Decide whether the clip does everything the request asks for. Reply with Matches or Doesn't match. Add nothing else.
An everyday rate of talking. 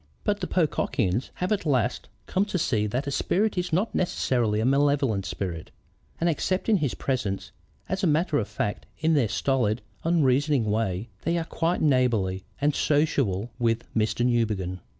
Matches